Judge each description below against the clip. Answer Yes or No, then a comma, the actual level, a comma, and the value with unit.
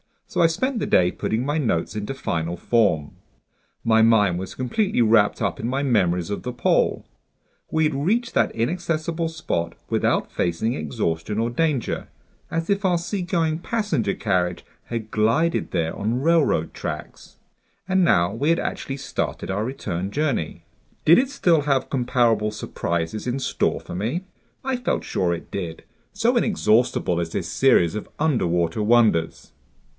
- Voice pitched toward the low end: Yes, low, 120 Hz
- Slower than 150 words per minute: No, average, 155 wpm